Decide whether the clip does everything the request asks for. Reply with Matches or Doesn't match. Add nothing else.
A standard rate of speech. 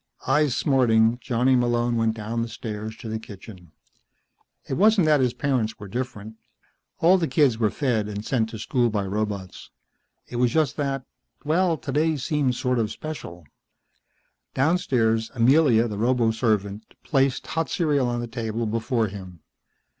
Matches